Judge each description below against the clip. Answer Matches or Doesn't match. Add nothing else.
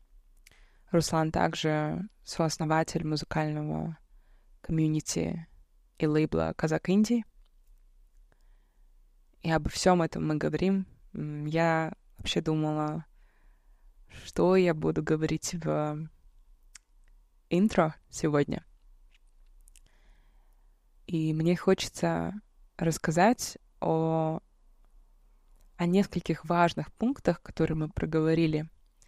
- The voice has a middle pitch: Matches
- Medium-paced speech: Doesn't match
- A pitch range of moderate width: Doesn't match